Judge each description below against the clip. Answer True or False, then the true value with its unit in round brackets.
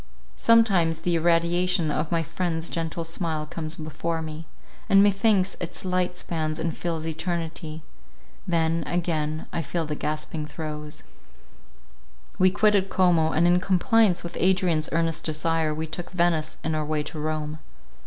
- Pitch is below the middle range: False (165 Hz)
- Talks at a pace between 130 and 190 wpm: True (145 wpm)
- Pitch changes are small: True (2.2 semitones)